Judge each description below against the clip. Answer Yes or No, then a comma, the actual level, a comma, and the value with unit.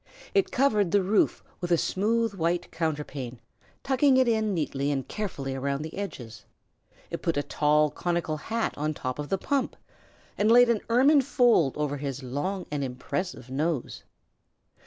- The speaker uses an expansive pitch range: Yes, wide, 7.4 semitones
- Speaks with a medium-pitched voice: Yes, medium, 170 Hz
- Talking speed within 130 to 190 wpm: Yes, average, 160 wpm